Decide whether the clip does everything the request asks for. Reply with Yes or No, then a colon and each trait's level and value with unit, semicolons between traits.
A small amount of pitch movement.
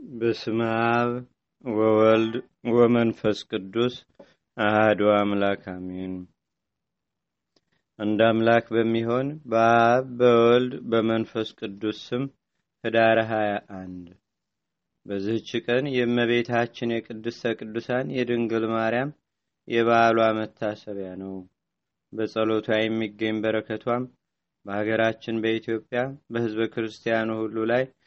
Yes: narrow, 1.4 semitones